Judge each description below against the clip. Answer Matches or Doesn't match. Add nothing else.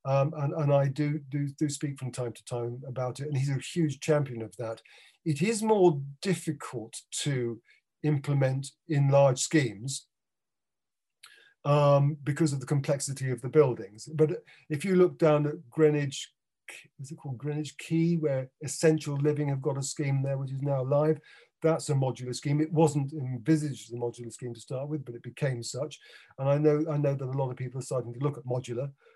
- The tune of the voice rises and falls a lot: Doesn't match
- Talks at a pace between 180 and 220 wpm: Matches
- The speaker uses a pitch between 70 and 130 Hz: Doesn't match